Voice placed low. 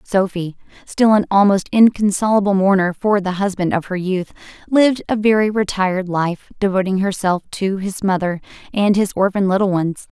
No: high, 195 Hz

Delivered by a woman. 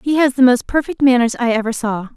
Yes: female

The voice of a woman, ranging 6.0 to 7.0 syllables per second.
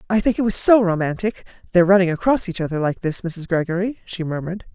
Yes: female; 6.2 syllables/s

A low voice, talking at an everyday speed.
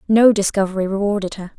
No: high, 200 Hz; average, 150 wpm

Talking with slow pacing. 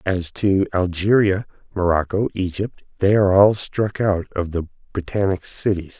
Yes: slow, 130 wpm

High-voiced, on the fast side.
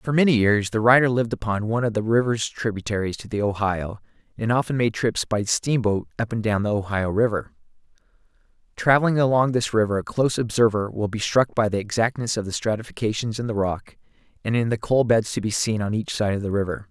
No: low, 110 Hz; fast, 215 wpm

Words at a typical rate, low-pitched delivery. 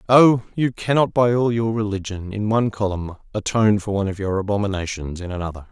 Yes: average, 190 wpm; low, 105 Hz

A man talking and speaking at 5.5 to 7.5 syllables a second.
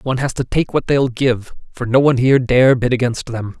Yes: male; 5.8 syllables/s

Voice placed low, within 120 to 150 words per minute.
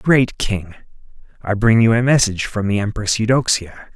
No: low, 110 Hz; average, 165 wpm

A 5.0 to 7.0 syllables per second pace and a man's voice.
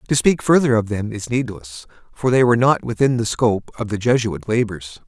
Yes: 5.5 syllables/s; male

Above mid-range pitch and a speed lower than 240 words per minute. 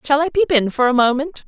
No: very high, 285 Hz; fast, 285 wpm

